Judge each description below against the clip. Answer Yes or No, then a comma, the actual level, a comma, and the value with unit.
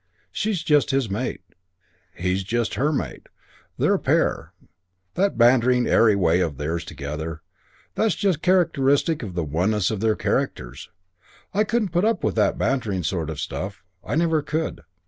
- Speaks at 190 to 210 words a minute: No, average, 155 wpm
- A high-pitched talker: No, low, 115 Hz